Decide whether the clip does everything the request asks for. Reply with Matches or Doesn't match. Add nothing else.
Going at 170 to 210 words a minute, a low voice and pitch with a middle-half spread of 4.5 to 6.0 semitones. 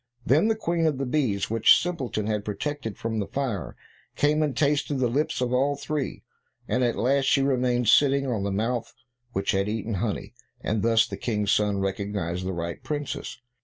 Matches